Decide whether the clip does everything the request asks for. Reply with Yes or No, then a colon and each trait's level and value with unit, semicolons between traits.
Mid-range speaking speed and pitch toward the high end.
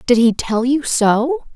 Yes: average, 195 wpm; very high, 250 Hz